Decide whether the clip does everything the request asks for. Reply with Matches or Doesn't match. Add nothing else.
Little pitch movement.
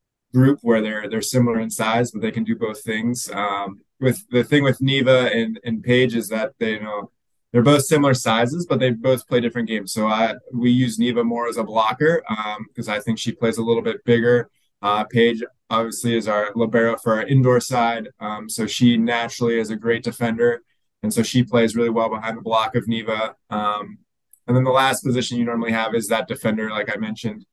Matches